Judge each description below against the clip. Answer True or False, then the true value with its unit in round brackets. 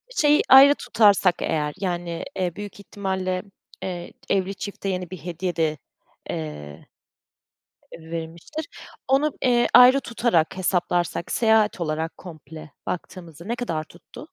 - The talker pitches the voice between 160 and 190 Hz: True (185 Hz)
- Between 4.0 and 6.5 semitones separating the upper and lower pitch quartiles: True (4.3 semitones)